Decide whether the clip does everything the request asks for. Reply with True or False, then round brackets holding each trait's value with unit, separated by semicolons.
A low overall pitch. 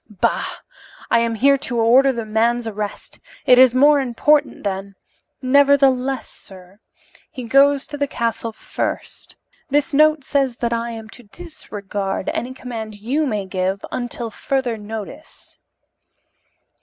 False (240 Hz)